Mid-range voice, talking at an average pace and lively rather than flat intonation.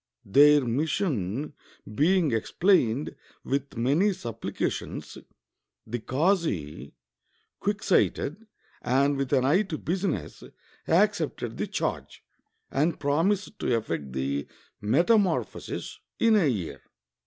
No: medium, 145 Hz; slow, 105 wpm; wide, 7.9 semitones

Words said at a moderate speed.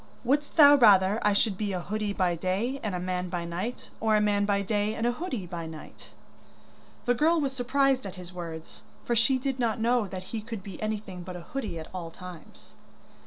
No: fast, 215 wpm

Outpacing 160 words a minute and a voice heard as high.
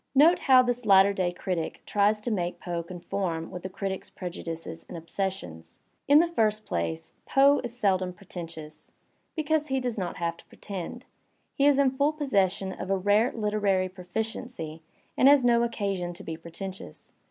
Yes: average, 175 wpm; high, 195 Hz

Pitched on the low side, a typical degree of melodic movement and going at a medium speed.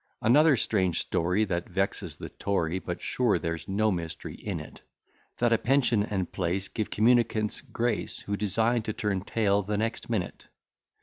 Yes: low, 105 Hz; average, 3.5 semitones; average, 165 wpm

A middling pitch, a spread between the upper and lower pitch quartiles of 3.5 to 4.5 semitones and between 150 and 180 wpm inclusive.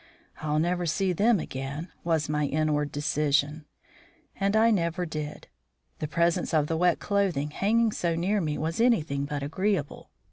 Yes: medium, 165 Hz; average, 4.1 semitones; average, 155 wpm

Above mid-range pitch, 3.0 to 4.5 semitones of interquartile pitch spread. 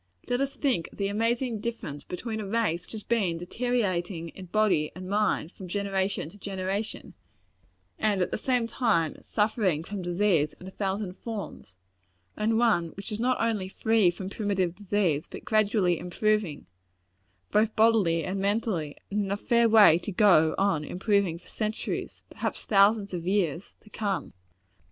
Yes: high, 200 Hz; average, 3.4 semitones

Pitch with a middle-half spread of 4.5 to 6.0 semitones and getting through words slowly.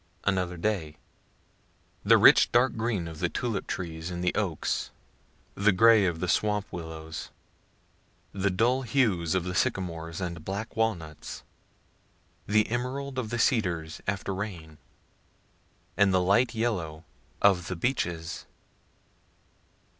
Yes: average, 4.9 semitones; slow, 125 wpm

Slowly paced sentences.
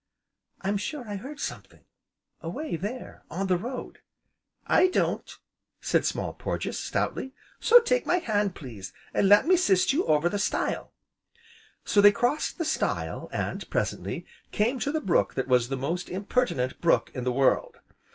No: average, 160 wpm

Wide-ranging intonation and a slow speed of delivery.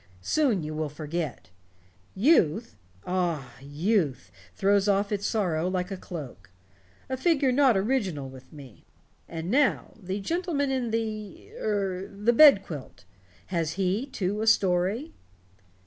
Yes: wide, 5.9 semitones; slow, 130 wpm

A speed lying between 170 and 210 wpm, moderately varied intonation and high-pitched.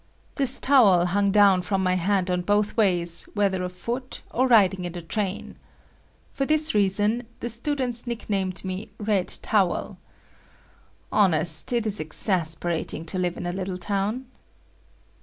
No: average, 140 wpm; average, 3.5 semitones; high, 195 Hz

